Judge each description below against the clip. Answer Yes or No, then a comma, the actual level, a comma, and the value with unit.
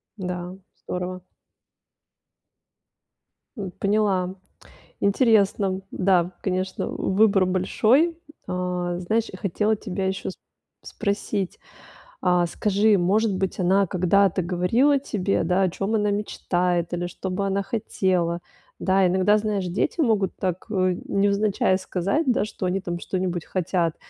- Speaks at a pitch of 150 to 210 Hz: Yes, high, 190 Hz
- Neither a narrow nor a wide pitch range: No, narrow, 2.1 semitones